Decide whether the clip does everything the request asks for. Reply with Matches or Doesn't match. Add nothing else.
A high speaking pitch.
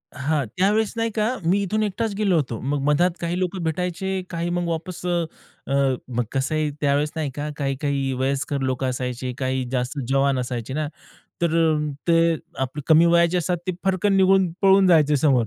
Doesn't match